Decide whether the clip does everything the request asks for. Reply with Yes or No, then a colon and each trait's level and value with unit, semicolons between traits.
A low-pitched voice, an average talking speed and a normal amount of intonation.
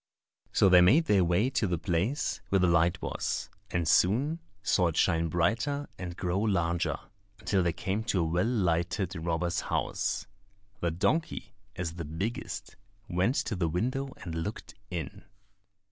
Yes: very low, 90 Hz; average, 160 wpm; average, 4.1 semitones